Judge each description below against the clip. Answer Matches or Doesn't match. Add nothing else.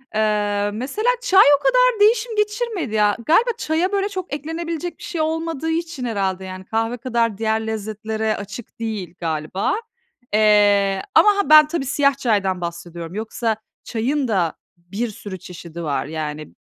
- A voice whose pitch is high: Matches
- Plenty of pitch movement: Matches